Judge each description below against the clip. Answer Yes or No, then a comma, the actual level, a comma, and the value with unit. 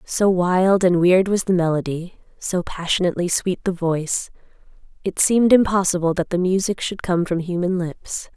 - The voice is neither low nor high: Yes, medium, 180 Hz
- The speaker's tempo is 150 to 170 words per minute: Yes, average, 165 wpm